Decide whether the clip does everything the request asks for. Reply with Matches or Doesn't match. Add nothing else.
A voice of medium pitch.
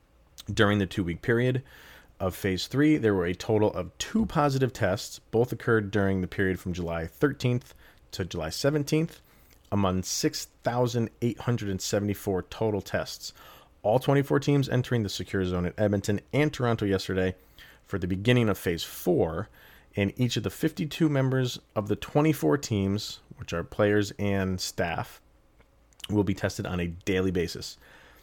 Doesn't match